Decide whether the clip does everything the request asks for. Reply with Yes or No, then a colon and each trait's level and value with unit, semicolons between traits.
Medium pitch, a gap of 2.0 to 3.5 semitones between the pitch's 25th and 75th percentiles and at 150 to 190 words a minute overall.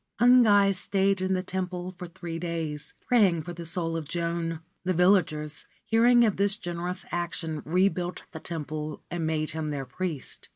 Yes: medium, 175 Hz; average, 2.7 semitones; average, 165 wpm